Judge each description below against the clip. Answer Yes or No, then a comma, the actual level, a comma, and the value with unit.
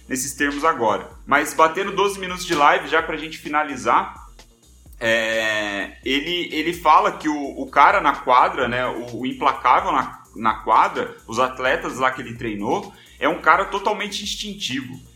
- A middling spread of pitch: No, wide, 6.0 semitones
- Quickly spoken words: No, average, 165 wpm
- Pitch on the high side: No, medium, 150 Hz